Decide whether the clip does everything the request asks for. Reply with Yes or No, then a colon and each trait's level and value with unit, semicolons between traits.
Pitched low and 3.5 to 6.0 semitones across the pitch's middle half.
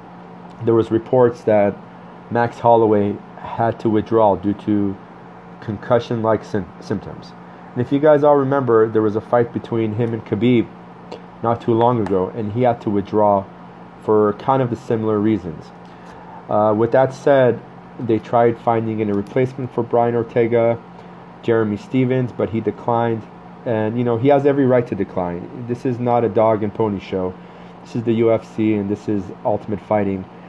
No: low, 110 Hz; average, 2.8 semitones